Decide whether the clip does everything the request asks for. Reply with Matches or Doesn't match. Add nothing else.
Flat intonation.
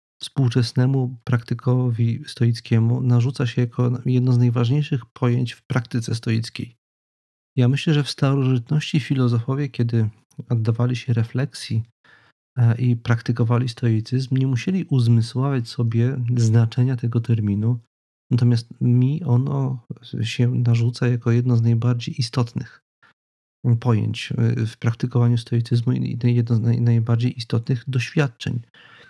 Matches